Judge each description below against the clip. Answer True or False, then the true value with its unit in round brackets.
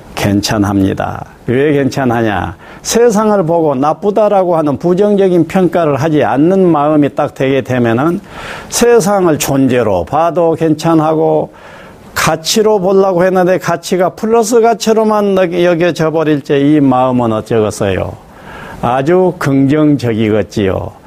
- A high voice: False (160 Hz)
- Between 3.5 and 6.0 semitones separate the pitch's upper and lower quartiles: True (5.6 semitones)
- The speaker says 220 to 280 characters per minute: True (275 characters per minute)